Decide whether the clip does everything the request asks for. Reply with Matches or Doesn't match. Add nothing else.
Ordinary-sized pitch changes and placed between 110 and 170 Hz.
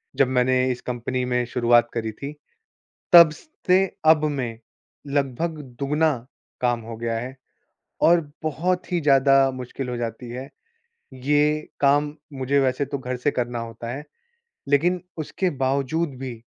Matches